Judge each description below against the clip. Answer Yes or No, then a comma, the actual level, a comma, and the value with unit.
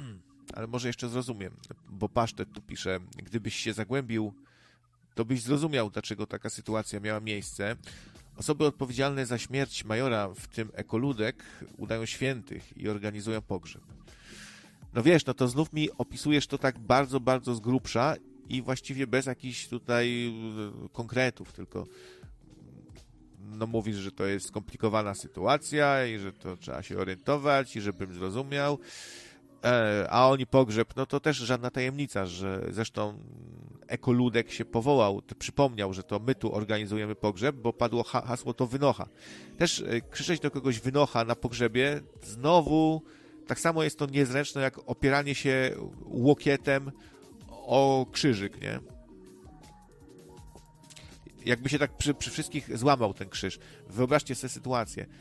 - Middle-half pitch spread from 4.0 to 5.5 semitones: Yes, average, 4.3 semitones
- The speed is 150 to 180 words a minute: No, average, 135 wpm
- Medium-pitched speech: No, low, 120 Hz